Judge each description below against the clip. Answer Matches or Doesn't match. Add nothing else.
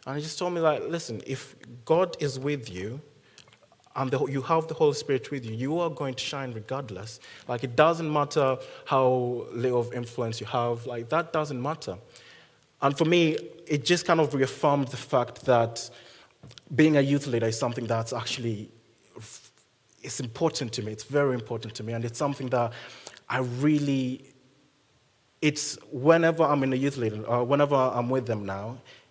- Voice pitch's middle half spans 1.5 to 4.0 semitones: Matches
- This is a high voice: Doesn't match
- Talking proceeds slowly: Doesn't match